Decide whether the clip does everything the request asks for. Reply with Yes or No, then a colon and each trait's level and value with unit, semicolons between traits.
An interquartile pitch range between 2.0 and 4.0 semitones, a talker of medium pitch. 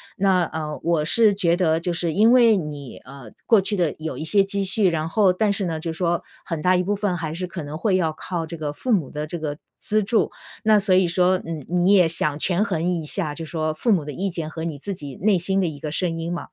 Yes: average, 3.6 semitones; medium, 175 Hz